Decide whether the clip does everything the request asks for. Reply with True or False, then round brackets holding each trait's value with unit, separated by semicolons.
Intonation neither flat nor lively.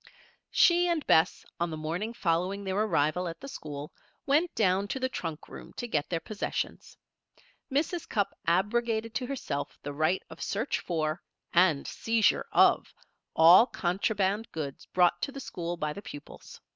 False (5.7 semitones)